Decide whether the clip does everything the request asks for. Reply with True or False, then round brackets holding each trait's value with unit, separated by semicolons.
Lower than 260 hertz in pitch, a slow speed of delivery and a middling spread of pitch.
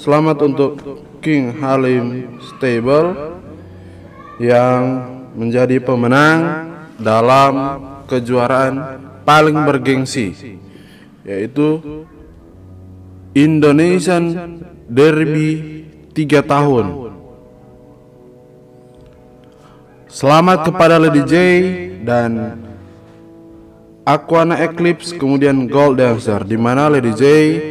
True (140 Hz; 65 wpm; 4.6 semitones)